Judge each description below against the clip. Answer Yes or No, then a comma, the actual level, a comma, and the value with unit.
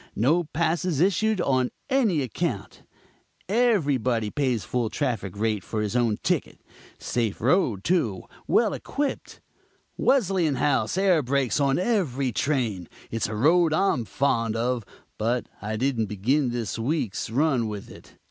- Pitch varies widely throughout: Yes, wide, 6.4 semitones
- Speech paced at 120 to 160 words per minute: Yes, slow, 135 wpm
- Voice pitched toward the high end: No, low, 130 Hz